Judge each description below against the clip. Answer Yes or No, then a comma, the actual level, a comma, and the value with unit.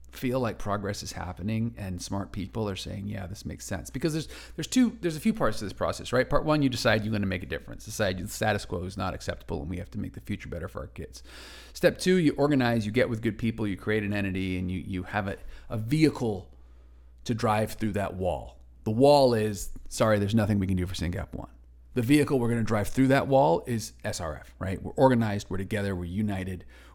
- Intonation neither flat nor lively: Yes, average, 4.2 semitones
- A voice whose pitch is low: Yes, low, 105 Hz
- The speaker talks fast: Yes, fast, 240 wpm